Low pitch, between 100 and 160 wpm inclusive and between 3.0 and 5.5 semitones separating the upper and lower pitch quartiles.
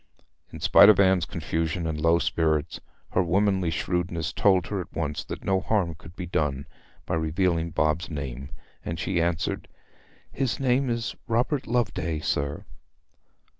Yes: very low, 85 Hz; average, 150 wpm; average, 3.5 semitones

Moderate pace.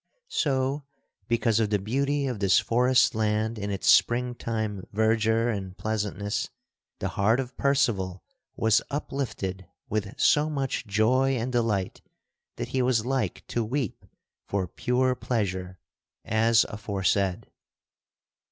No: slow, 125 wpm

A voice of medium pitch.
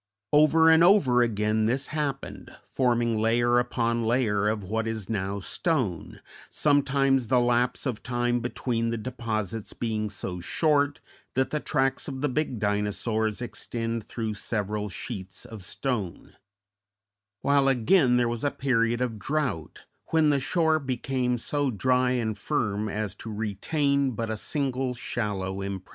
No: low, 120 Hz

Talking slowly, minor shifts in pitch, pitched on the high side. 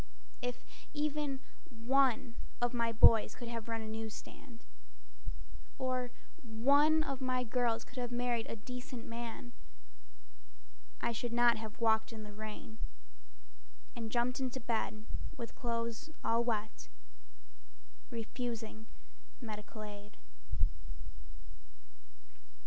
Yes: slow, 110 wpm; narrow, 2.1 semitones; high, 235 Hz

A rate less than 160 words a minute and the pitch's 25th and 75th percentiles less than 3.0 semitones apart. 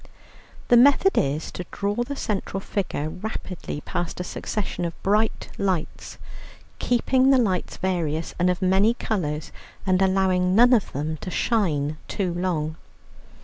No: average, 145 wpm; average, 4.3 semitones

